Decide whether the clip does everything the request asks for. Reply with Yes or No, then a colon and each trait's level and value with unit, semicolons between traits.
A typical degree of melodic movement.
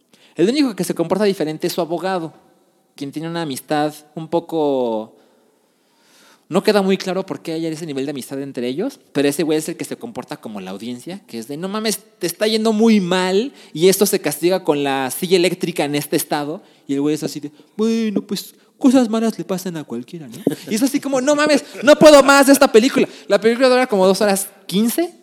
No: wide, 6.3 semitones